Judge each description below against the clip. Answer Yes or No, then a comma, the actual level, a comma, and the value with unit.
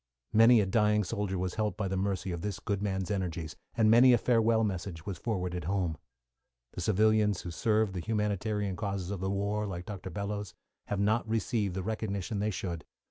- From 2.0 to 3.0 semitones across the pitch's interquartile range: Yes, narrow, 2.5 semitones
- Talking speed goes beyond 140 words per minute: Yes, average, 190 wpm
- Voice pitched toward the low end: Yes, low, 100 Hz